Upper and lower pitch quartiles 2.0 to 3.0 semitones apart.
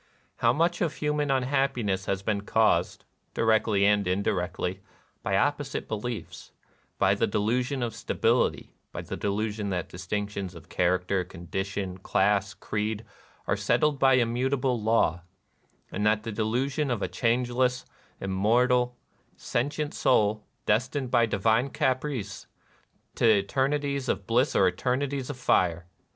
No: average, 4.5 semitones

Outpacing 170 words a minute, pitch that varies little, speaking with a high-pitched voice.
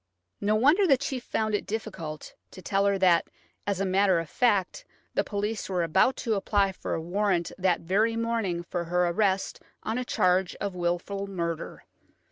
No: average, 180 wpm; average, 3.5 semitones; high, 195 Hz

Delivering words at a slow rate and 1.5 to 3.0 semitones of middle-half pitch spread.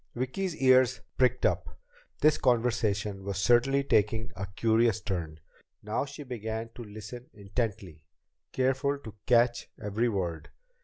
No: slow, 120 wpm; average, 3.8 semitones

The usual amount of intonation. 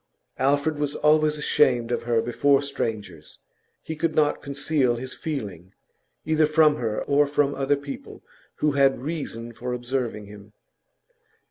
Yes: average, 3.9 semitones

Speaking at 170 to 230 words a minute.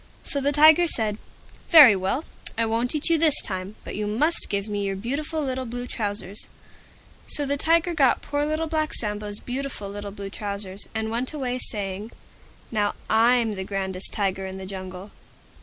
Yes: average, 175 wpm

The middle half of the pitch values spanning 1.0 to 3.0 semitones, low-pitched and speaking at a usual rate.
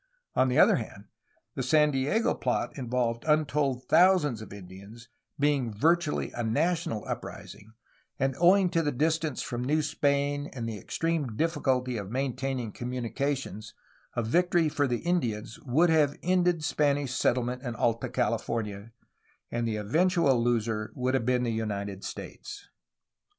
No: average, 4.7 semitones; low, 130 Hz; average, 150 wpm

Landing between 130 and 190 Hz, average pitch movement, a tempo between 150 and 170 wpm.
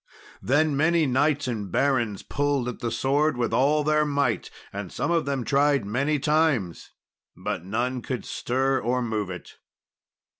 Yes: low, 135 Hz; average, 3.8 semitones; average, 155 wpm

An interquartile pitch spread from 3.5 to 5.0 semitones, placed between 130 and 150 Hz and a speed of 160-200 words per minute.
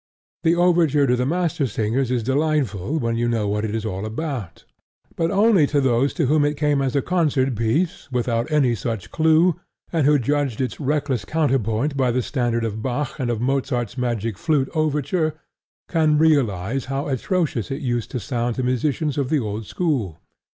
Yes: average, 4.5 semitones; low, 135 Hz; average, 180 wpm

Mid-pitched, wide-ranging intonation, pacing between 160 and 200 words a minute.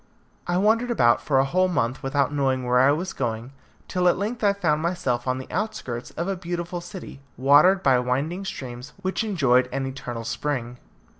Yes: medium, 145 Hz; wide, 6.3 semitones; average, 190 wpm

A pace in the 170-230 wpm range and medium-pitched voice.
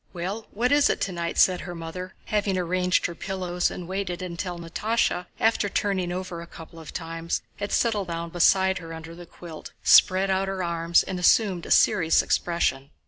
Yes: average, 185 wpm; medium, 180 Hz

